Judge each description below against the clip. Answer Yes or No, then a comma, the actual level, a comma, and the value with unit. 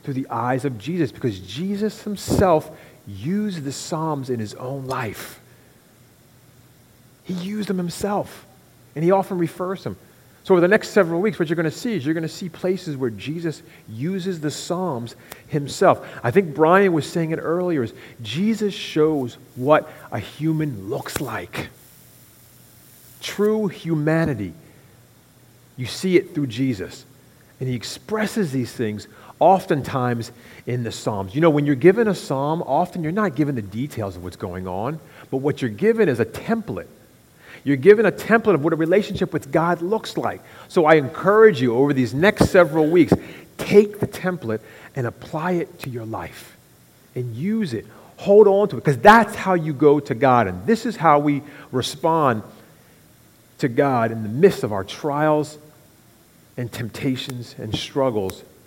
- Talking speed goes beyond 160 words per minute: Yes, average, 170 wpm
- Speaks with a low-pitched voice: No, medium, 150 Hz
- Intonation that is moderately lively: No, wide, 6.4 semitones